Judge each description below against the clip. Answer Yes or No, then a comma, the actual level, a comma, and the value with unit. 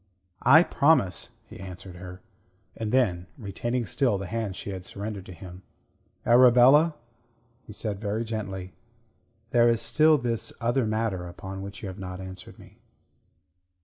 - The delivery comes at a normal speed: Yes, average, 145 wpm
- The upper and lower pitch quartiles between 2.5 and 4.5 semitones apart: Yes, average, 4.1 semitones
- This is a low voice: Yes, low, 105 Hz